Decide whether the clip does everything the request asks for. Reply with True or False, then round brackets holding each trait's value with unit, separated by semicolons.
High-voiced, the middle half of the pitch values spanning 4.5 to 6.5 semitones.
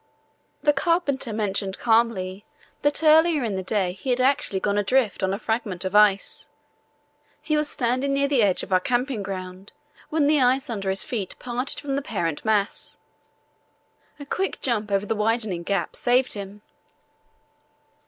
True (225 Hz; 5.6 semitones)